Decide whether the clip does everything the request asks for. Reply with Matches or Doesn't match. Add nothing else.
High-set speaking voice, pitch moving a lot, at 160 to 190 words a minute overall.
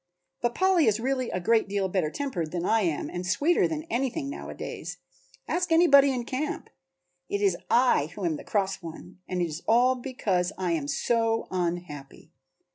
Matches